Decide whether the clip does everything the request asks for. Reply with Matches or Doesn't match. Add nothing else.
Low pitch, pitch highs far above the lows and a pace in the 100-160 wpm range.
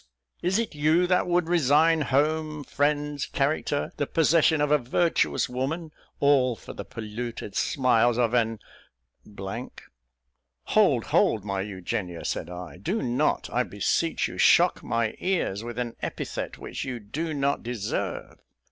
Matches